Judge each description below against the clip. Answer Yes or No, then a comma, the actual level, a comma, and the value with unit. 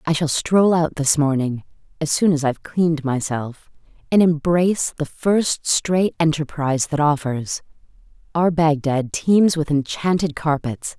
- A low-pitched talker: No, medium, 155 Hz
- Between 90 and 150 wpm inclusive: Yes, average, 140 wpm